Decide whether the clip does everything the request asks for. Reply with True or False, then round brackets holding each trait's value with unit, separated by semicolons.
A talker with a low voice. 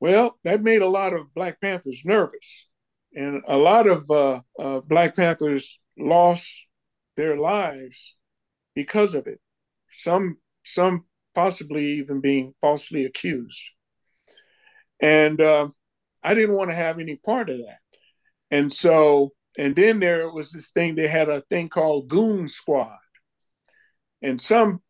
False (170 Hz)